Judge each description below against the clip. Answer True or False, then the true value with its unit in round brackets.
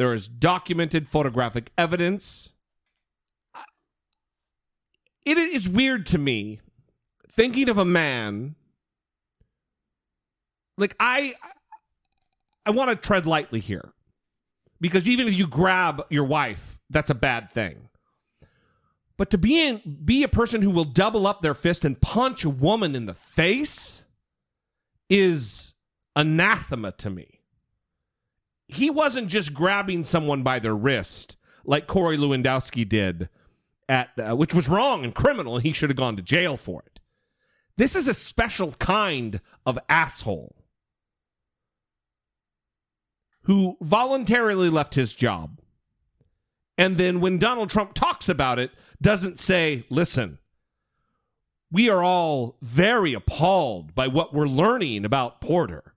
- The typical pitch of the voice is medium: True (165 Hz)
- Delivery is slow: True (125 wpm)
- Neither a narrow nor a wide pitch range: False (7.8 semitones)